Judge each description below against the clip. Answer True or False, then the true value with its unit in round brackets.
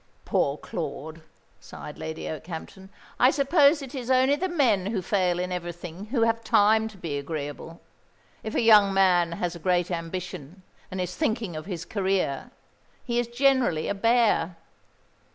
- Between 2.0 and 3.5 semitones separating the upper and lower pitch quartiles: False (5.4 semitones)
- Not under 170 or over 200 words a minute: False (160 wpm)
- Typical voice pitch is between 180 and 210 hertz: True (190 Hz)